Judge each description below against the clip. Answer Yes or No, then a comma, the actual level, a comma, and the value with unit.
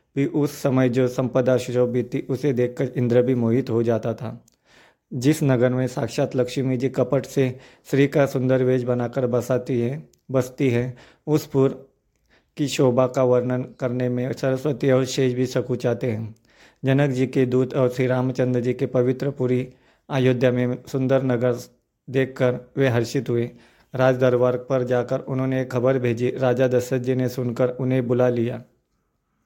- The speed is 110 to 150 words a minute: No, average, 165 wpm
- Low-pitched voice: Yes, low, 130 Hz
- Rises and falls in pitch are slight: Yes, narrow, 1.2 semitones